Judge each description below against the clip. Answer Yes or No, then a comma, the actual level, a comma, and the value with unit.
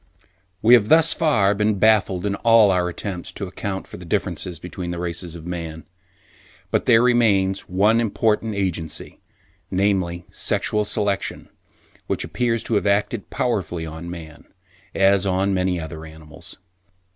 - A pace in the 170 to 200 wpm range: No, average, 145 wpm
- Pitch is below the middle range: Yes, very low, 95 Hz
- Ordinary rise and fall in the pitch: Yes, average, 3.4 semitones